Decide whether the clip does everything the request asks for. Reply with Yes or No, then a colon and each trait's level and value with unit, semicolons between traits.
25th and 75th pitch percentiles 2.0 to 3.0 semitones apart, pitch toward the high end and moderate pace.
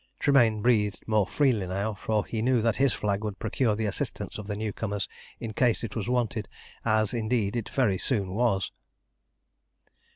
No: narrow, 2.5 semitones; low, 110 Hz; average, 175 wpm